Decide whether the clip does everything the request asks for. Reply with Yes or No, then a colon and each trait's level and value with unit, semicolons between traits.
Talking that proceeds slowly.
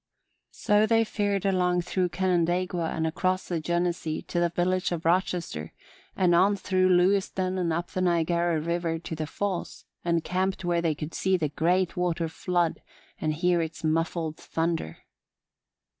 No: average, 160 wpm